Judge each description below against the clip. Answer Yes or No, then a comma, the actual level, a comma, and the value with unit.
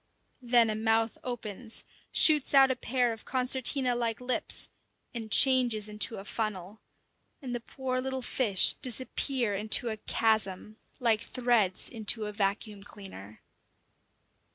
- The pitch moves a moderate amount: Yes, average, 3.1 semitones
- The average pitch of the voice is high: Yes, high, 230 Hz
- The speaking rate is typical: No, slow, 130 wpm